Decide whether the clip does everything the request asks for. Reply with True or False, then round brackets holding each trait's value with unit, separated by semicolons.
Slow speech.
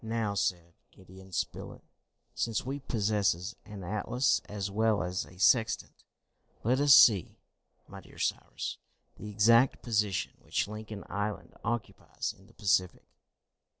True (130 wpm)